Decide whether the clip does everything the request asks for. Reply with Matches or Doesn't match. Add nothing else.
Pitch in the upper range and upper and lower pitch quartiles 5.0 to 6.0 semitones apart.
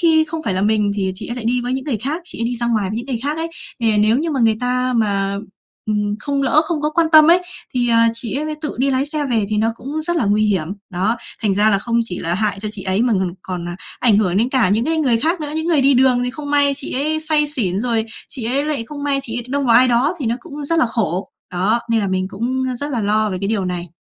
Matches